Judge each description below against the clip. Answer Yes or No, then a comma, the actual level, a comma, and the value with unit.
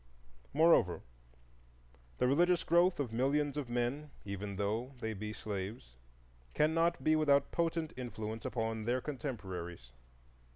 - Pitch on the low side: Yes, low, 125 Hz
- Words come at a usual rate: No, slow, 120 wpm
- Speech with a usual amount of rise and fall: No, wide, 6.0 semitones